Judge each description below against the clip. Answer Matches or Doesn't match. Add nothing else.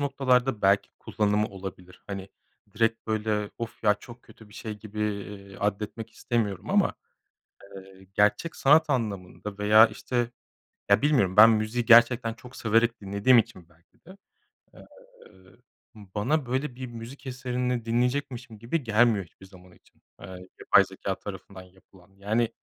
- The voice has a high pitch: Doesn't match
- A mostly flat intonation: Doesn't match